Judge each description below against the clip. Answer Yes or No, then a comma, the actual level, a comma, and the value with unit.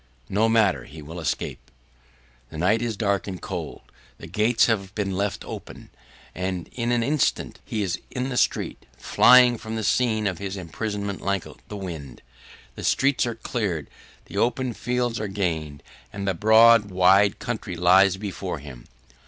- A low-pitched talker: Yes, low, 100 Hz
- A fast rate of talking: No, average, 165 wpm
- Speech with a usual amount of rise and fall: Yes, average, 3.8 semitones